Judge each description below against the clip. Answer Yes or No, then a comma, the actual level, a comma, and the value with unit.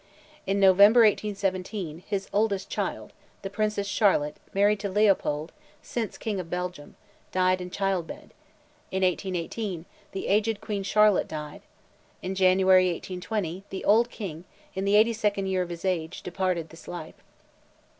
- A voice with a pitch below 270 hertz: Yes, high, 190 Hz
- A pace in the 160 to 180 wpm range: No, average, 145 wpm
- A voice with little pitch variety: Yes, narrow, 2.3 semitones